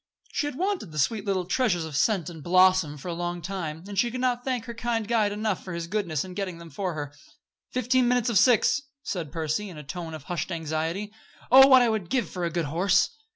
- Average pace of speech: No, fast, 240 wpm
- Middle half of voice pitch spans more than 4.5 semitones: Yes, wide, 5.6 semitones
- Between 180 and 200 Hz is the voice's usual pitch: Yes, medium, 185 Hz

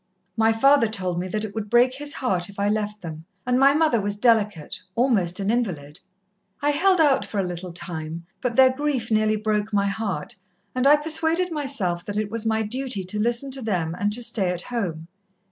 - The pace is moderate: No, fast, 210 wpm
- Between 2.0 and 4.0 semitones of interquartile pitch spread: No, wide, 5.4 semitones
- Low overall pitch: No, high, 215 Hz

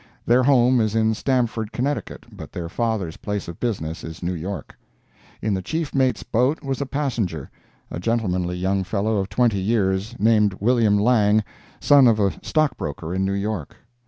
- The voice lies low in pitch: Yes, low, 105 Hz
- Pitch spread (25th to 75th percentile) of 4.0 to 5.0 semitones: Yes, average, 4.4 semitones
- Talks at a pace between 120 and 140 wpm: No, average, 165 wpm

